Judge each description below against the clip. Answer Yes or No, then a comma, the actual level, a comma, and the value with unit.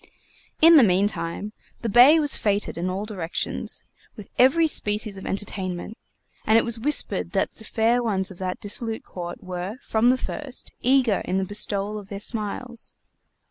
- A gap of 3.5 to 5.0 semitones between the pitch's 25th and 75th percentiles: Yes, average, 3.9 semitones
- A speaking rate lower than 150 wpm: No, average, 170 wpm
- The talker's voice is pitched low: No, high, 210 Hz